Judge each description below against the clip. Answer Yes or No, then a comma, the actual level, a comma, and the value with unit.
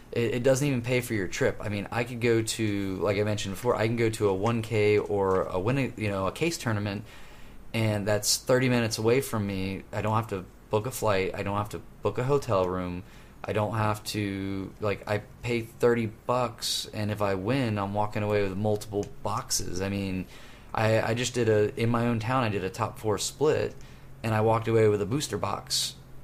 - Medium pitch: No, low, 105 Hz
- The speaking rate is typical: No, fast, 220 wpm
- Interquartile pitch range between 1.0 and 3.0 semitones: Yes, average, 2.7 semitones